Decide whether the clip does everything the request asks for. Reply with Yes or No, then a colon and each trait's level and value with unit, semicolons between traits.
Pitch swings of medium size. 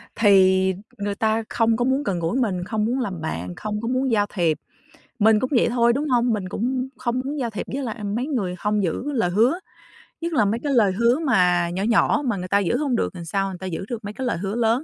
Yes: average, 4.6 semitones